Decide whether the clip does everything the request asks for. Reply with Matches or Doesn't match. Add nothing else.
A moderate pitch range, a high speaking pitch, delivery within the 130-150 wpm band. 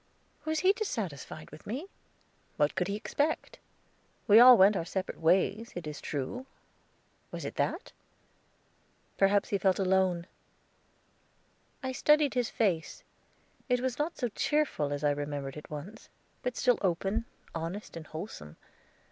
Doesn't match